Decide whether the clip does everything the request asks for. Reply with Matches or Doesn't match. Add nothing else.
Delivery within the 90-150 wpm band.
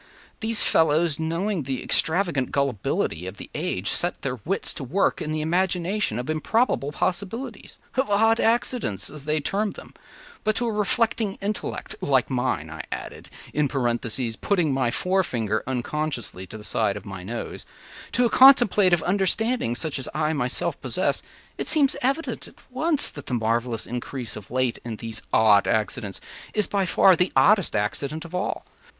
Doesn't match